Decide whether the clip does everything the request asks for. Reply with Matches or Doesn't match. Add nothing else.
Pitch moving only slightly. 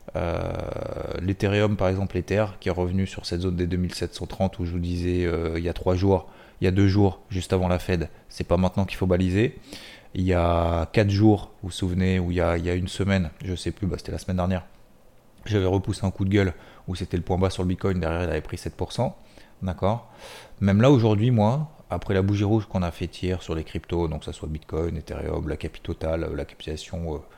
Matches